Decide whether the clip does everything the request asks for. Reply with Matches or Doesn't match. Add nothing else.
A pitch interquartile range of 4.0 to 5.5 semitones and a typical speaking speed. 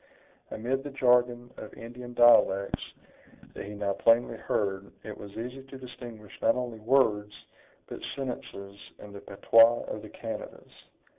Doesn't match